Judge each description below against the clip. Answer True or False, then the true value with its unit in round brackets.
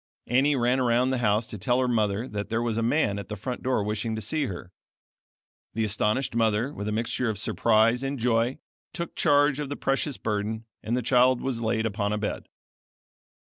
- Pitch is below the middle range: True (115 Hz)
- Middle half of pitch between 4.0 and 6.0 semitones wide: False (3.2 semitones)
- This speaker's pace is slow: False (205 wpm)